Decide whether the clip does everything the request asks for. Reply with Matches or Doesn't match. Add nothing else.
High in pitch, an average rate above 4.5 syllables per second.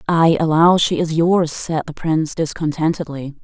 Doesn't match